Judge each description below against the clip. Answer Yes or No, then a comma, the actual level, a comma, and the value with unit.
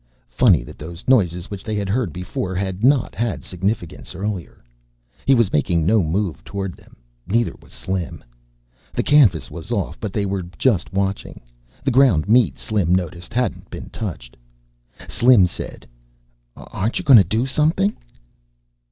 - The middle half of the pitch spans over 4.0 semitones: Yes, average, 4.7 semitones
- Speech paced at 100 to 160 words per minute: Yes, average, 155 wpm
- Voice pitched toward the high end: No, low, 100 Hz